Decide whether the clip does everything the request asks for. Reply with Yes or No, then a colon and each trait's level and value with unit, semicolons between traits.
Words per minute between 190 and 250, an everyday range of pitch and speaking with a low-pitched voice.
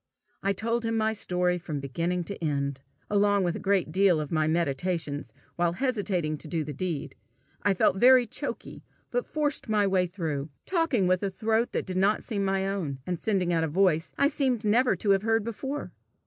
No: average, 200 wpm; average, 4.7 semitones; high, 190 Hz